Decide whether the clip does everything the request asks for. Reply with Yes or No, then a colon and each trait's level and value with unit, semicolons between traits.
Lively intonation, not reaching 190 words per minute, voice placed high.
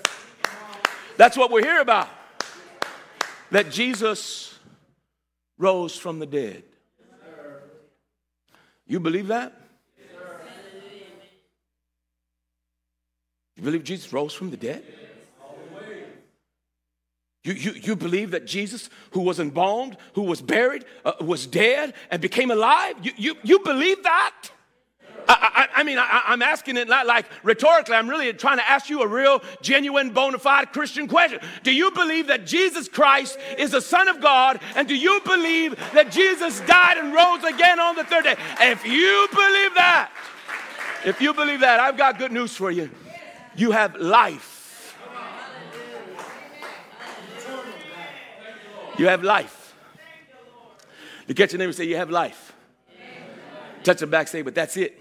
Yes: wide, 8.7 semitones; average, 140 wpm; high, 235 Hz